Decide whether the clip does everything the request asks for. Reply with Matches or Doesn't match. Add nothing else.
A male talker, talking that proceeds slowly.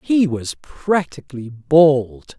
Matches